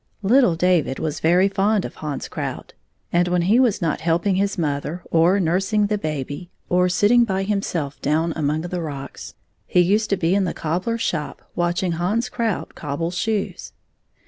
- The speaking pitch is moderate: Yes, medium, 180 Hz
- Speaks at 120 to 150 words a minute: No, average, 175 wpm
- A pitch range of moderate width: Yes, average, 3.7 semitones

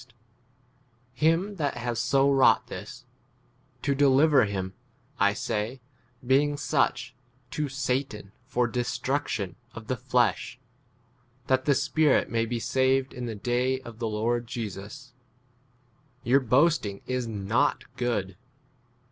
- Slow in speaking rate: Yes, slow, 125 wpm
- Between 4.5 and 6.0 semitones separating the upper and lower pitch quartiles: No, average, 3.3 semitones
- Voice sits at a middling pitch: No, low, 125 Hz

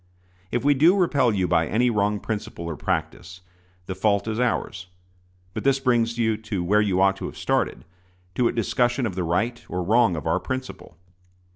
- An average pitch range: Yes, average, 4.8 semitones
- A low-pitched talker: Yes, low, 105 Hz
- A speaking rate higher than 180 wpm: Yes, average, 190 wpm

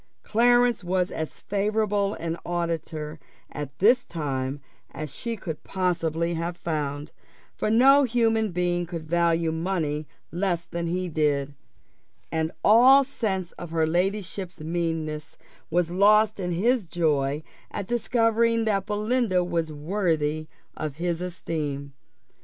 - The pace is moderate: No, slow, 125 wpm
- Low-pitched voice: No, medium, 175 Hz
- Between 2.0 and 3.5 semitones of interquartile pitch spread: No, average, 4.7 semitones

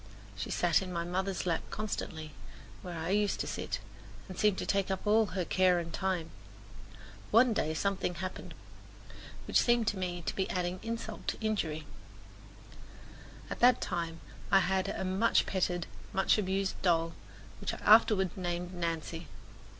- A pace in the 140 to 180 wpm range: Yes, average, 160 wpm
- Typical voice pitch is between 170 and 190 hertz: Yes, medium, 185 Hz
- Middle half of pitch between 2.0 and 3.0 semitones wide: Yes, narrow, 2.5 semitones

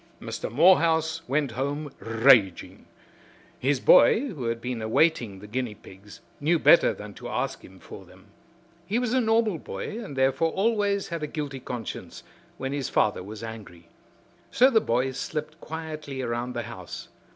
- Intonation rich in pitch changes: Yes, wide, 6.2 semitones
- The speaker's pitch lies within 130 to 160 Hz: Yes, low, 135 Hz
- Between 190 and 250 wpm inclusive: No, average, 160 wpm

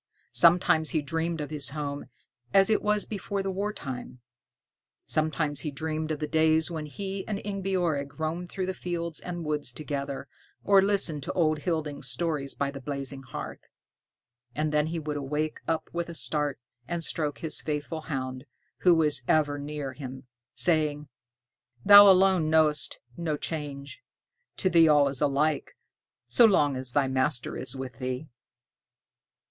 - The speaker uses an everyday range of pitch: Yes, average, 3.1 semitones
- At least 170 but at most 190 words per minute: No, average, 155 wpm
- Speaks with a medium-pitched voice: Yes, medium, 155 Hz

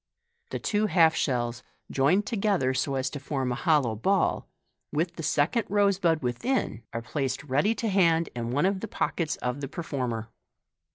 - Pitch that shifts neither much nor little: No, wide, 6.7 semitones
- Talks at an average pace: Yes, average, 175 wpm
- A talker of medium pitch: Yes, medium, 150 Hz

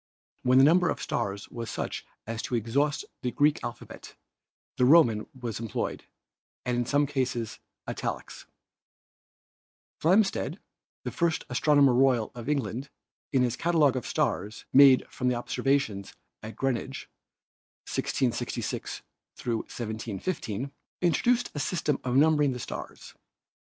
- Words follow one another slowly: Yes, slow, 125 wpm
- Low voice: Yes, low, 130 Hz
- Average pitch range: Yes, average, 3.9 semitones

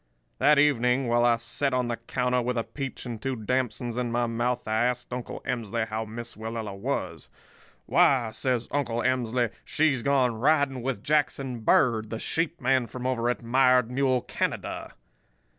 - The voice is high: No, low, 125 Hz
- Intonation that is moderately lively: No, narrow, 2.2 semitones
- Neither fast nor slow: Yes, average, 170 wpm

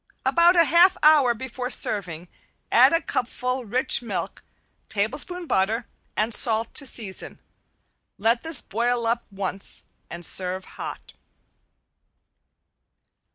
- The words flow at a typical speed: No, slow, 110 wpm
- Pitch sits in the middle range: No, high, 235 Hz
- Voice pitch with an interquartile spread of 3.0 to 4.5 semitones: No, average, 4.9 semitones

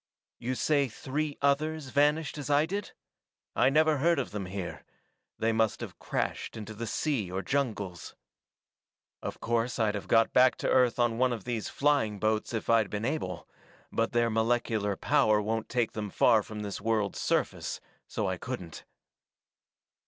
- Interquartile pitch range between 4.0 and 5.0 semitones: Yes, average, 4.6 semitones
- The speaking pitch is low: Yes, low, 115 Hz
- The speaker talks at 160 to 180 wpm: Yes, average, 165 wpm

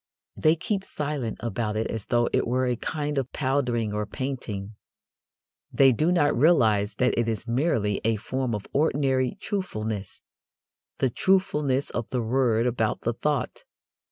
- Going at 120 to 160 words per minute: Yes, average, 155 wpm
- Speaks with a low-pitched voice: Yes, low, 125 Hz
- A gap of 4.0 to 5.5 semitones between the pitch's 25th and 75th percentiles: Yes, average, 4.5 semitones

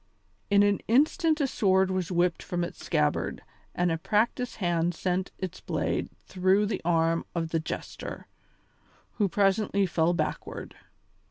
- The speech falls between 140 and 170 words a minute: Yes, average, 145 wpm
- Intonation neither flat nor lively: Yes, average, 3.0 semitones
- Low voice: No, medium, 185 Hz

